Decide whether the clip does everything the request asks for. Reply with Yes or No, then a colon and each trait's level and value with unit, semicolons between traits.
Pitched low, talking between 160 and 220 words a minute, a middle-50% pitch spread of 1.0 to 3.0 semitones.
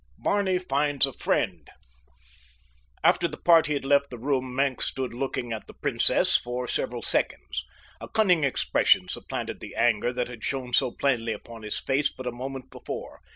Yes: low, 130 Hz; average, 170 wpm; average, 2.7 semitones